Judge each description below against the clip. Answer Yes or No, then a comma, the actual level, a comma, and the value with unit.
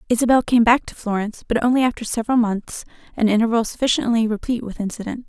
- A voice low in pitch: No, high, 230 Hz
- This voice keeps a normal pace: Yes, average, 180 wpm